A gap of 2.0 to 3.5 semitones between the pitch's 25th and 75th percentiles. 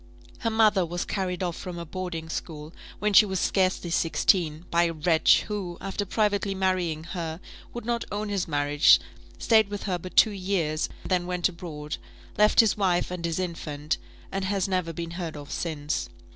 Yes: average, 3.1 semitones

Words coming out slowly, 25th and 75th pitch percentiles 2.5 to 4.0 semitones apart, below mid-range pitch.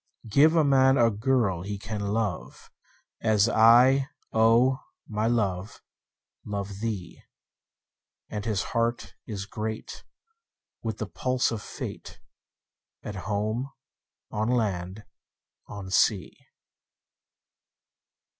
Yes: slow, 105 wpm; average, 2.8 semitones; low, 110 Hz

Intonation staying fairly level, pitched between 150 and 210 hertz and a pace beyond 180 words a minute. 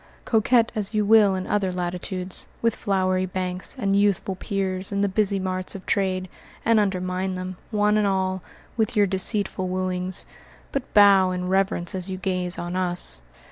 No: narrow, 1.7 semitones; high, 190 Hz; average, 170 wpm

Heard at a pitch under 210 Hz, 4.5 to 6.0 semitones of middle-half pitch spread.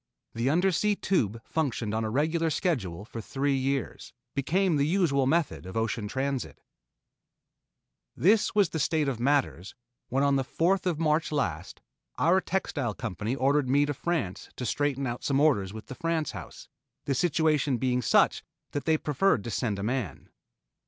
Yes: medium, 140 Hz; average, 5.2 semitones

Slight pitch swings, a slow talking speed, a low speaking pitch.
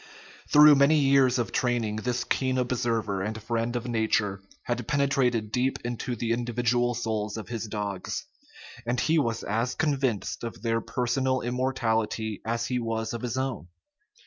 No: narrow, 2.3 semitones; average, 160 wpm; low, 120 Hz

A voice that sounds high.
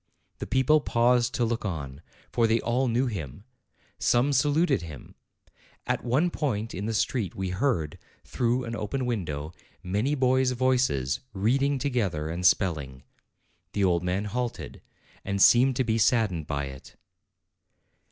No: low, 115 Hz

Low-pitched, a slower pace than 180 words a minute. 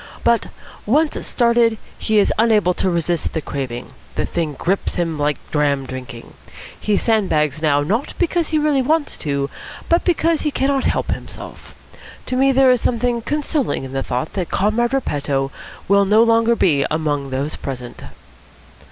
No: high, 200 Hz; average, 160 wpm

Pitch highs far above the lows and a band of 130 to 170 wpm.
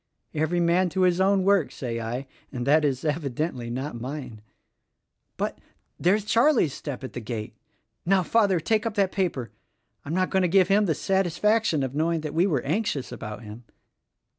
No: wide, 6.4 semitones; average, 185 wpm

